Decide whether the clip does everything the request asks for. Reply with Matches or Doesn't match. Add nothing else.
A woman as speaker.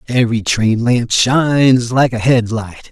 Doesn't match